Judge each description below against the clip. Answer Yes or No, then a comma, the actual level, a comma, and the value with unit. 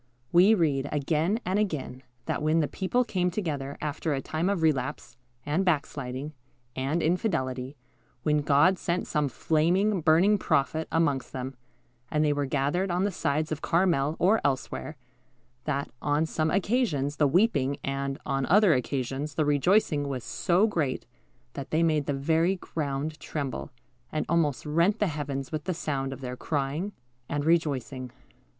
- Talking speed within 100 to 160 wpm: Yes, average, 155 wpm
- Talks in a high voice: No, medium, 150 Hz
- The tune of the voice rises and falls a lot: No, average, 3.8 semitones